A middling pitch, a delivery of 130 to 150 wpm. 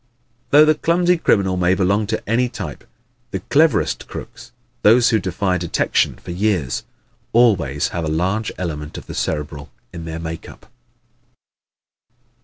No: very low, 95 Hz; average, 140 wpm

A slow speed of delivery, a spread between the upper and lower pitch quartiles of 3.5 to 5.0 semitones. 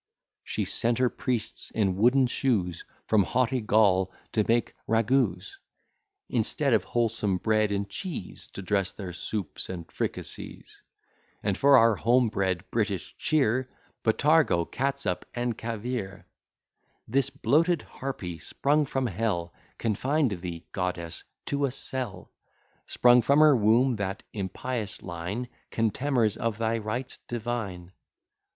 Yes: slow, 125 wpm; average, 4.6 semitones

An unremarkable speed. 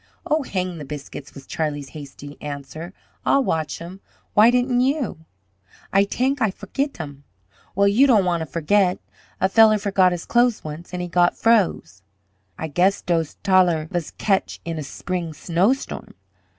Yes: average, 165 wpm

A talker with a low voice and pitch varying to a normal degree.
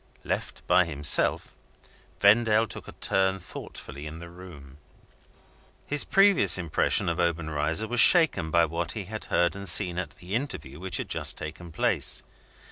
Yes: very low, 90 Hz; average, 4.4 semitones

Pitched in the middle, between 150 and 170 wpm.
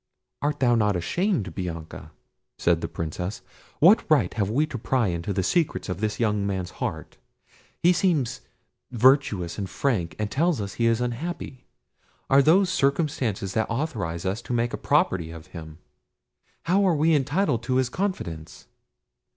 No: low, 115 Hz; average, 160 wpm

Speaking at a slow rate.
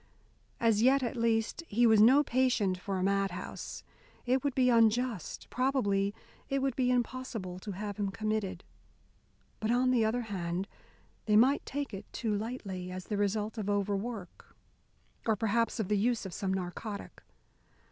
No: average, 165 wpm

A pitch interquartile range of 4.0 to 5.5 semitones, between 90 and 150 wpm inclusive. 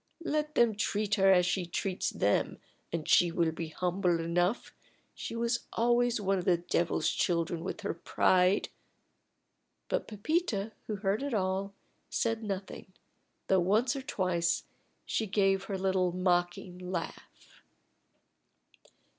No: average, 3.4 semitones; slow, 135 wpm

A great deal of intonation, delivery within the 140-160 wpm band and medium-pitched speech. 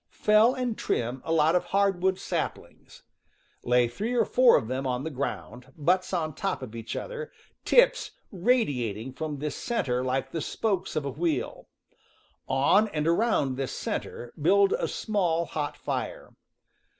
Yes: wide, 7.3 semitones; average, 155 wpm; medium, 160 Hz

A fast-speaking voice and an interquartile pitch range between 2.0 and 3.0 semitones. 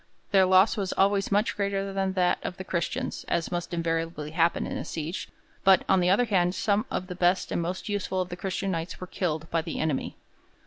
Yes: fast, 220 wpm; narrow, 2.5 semitones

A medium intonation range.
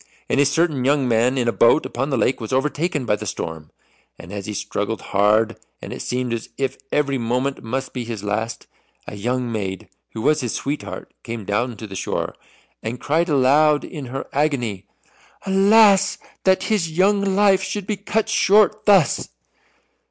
No: wide, 6.1 semitones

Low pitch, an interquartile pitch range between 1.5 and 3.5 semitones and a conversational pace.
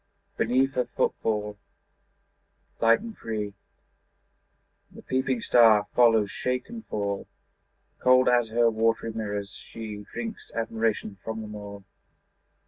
No: low, 115 Hz; average, 2.7 semitones; slow, 115 wpm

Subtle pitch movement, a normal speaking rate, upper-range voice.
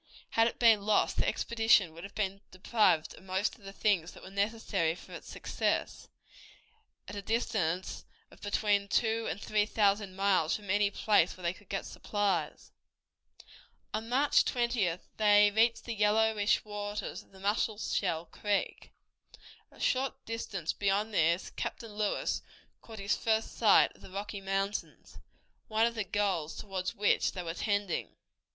Yes: narrow, 2.3 semitones; average, 160 wpm; high, 205 Hz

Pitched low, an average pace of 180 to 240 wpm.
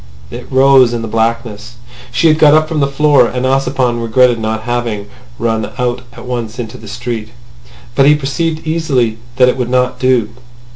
Yes: low, 125 Hz; average, 185 wpm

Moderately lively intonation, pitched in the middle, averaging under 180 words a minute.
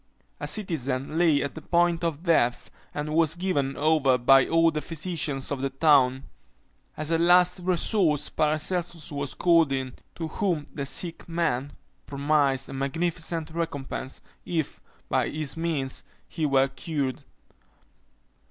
Yes: average, 3.5 semitones; medium, 155 Hz; average, 140 wpm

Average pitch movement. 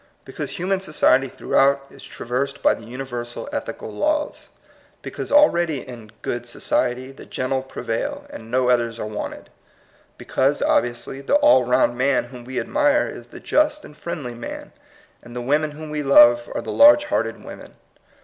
No: wide, 5.9 semitones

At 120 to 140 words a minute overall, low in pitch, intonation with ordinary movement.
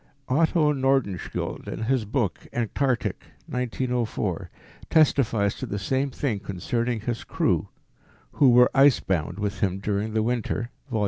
Yes: slow, 135 wpm; low, 120 Hz; average, 4.3 semitones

